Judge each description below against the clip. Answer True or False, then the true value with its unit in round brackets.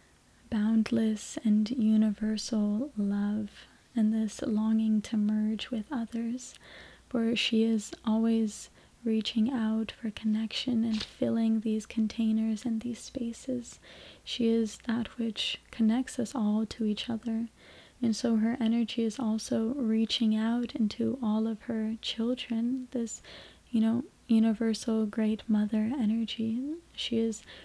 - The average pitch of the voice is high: True (225 Hz)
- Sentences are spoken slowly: True (125 wpm)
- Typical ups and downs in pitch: False (1.3 semitones)